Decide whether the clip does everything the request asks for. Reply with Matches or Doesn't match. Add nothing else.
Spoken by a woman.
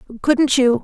Matches